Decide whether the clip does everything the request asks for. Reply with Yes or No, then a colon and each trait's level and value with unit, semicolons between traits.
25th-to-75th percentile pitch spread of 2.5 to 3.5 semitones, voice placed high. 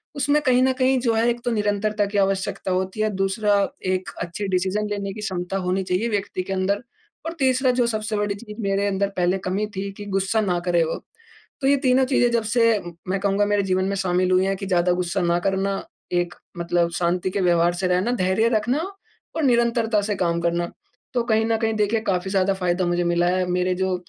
Yes: average, 3.2 semitones; high, 195 Hz